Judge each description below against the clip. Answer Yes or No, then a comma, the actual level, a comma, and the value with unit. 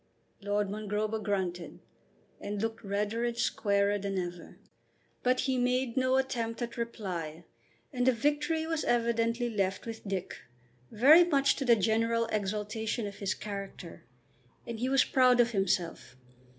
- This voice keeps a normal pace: Yes, average, 145 wpm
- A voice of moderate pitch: No, high, 225 Hz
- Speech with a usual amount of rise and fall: Yes, average, 3.6 semitones